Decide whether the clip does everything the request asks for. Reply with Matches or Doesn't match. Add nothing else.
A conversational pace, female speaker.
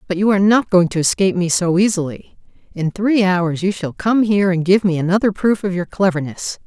Doesn't match